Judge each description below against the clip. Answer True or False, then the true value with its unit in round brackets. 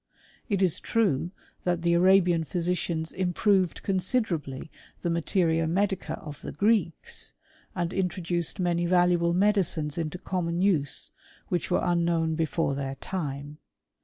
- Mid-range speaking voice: True (175 Hz)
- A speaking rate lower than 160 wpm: True (135 wpm)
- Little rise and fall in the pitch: True (2.3 semitones)